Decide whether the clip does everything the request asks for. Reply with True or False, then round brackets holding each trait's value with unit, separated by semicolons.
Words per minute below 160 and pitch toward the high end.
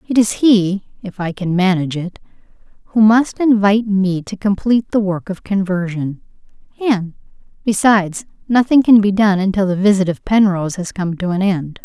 False (165 wpm; 200 Hz)